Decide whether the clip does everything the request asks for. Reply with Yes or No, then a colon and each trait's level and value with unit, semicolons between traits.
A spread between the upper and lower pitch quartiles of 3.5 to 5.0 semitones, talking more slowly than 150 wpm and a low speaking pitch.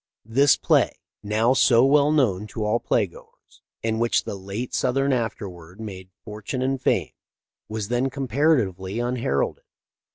Yes: average, 4.3 semitones; average, 140 wpm; low, 115 Hz